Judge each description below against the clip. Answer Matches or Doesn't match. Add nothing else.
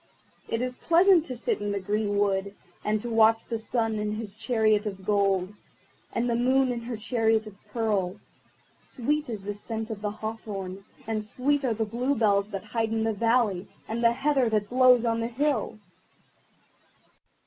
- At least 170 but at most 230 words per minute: Matches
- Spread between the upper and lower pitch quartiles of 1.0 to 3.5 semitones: Matches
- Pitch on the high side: Matches